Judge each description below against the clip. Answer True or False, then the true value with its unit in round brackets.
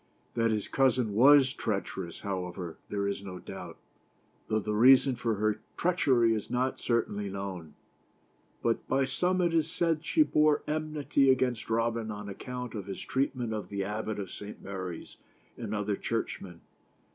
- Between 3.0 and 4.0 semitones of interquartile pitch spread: False (4.7 semitones)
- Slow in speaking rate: False (165 wpm)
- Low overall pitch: True (115 Hz)